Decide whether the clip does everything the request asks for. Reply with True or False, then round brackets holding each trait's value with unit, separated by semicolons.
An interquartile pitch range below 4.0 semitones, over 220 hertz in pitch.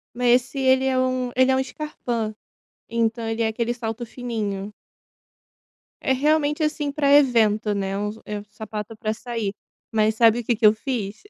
True (3.2 semitones; 235 Hz)